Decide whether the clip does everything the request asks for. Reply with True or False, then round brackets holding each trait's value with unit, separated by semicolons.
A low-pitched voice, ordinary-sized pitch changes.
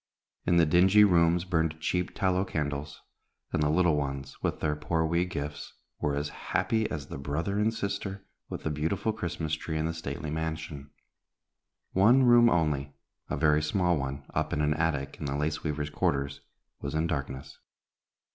True (80 Hz; 3.2 semitones)